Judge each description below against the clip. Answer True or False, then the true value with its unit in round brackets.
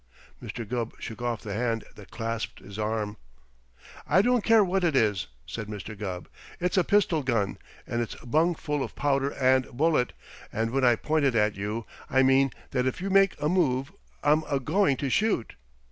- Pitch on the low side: True (130 Hz)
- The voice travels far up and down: True (5.8 semitones)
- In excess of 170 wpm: True (190 wpm)